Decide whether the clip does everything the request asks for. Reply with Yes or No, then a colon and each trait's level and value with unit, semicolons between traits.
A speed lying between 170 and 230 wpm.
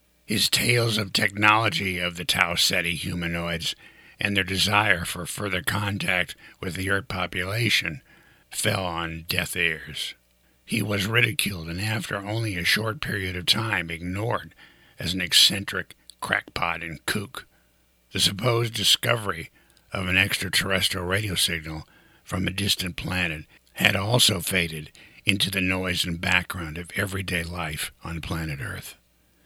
No: slow, 135 wpm